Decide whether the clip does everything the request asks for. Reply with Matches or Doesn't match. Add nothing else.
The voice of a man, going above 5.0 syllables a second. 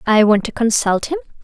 Doesn't match